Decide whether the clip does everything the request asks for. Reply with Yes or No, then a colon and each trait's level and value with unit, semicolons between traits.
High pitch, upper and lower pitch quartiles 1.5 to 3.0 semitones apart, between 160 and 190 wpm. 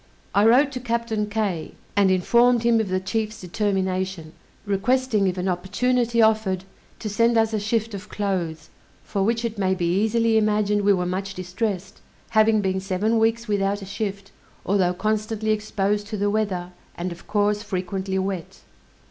Yes: high, 205 Hz; average, 2.7 semitones; average, 165 wpm